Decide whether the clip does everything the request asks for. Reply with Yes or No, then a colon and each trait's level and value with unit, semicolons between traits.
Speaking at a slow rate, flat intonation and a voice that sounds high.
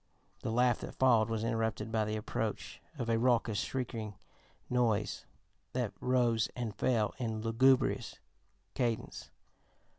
No: slow, 130 wpm; narrow, 2.1 semitones; low, 115 Hz